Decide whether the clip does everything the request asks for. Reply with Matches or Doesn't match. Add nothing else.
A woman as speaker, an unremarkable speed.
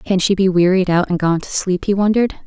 Doesn't match